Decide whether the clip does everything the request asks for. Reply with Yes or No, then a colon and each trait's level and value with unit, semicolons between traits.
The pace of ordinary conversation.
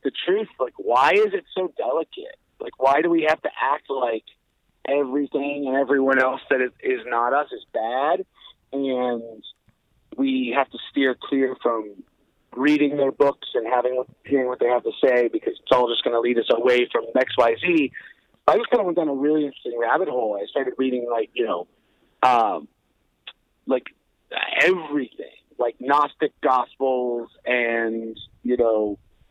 Yes: average, 165 wpm